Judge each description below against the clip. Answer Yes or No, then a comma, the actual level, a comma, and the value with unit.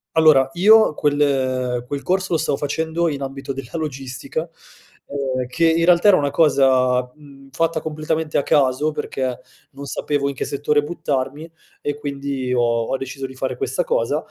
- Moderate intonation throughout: Yes, average, 3.1 semitones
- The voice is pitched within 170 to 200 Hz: No, medium, 140 Hz